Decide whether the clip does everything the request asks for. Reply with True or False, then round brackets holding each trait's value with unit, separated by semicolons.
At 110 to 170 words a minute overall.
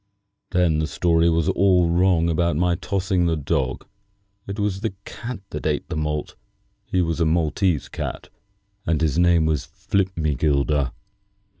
True (150 wpm)